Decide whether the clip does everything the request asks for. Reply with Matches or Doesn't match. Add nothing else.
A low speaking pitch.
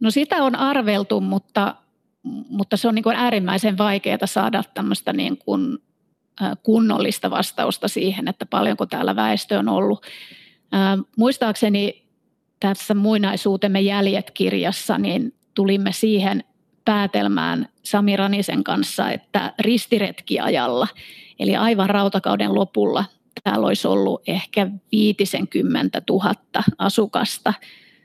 Doesn't match